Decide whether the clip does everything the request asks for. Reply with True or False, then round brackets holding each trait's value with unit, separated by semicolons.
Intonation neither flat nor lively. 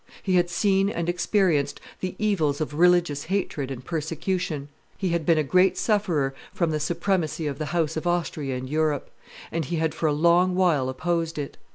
True (3.2 semitones)